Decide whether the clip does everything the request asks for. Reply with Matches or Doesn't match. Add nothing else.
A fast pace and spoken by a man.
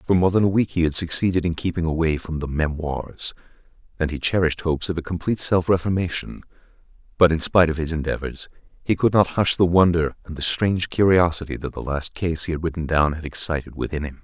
Matches